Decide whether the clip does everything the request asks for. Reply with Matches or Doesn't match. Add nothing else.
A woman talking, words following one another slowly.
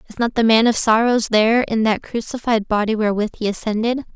Doesn't match